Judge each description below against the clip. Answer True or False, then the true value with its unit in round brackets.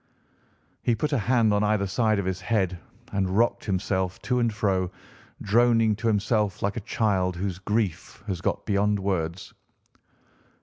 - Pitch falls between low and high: False (100 Hz)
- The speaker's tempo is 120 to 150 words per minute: False (160 wpm)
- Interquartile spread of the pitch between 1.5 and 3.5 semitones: True (2.8 semitones)